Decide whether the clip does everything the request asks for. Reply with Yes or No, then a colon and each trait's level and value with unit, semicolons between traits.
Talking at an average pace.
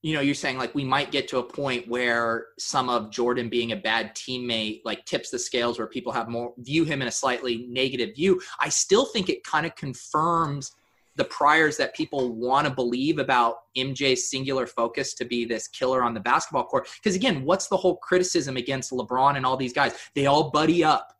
No: fast, 215 wpm